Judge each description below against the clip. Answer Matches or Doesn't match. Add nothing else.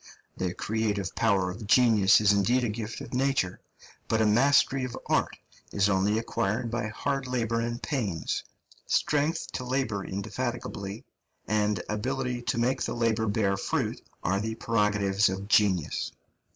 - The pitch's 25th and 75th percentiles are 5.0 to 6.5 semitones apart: Doesn't match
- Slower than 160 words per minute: Matches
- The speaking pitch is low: Matches